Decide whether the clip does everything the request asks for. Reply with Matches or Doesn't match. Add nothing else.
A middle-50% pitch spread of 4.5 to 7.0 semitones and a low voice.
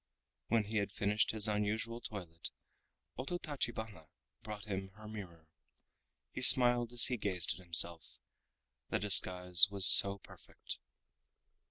Doesn't match